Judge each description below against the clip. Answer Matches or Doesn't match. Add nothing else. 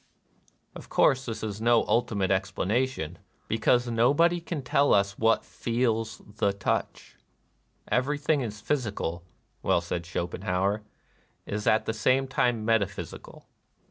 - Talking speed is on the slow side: Matches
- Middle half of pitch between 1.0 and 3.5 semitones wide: Doesn't match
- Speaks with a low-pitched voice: Matches